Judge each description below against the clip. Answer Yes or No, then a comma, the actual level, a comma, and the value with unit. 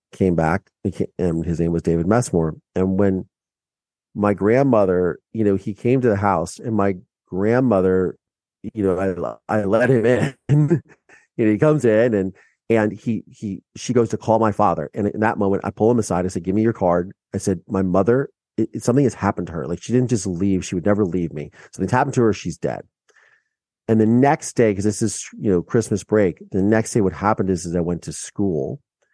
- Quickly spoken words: Yes, fast, 220 wpm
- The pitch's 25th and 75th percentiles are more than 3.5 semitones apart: No, average, 3.2 semitones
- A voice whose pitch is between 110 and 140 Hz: No, low, 100 Hz